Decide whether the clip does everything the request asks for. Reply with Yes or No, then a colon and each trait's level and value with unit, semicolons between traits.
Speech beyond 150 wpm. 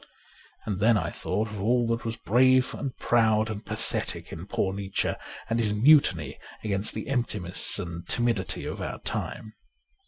Yes: average, 160 wpm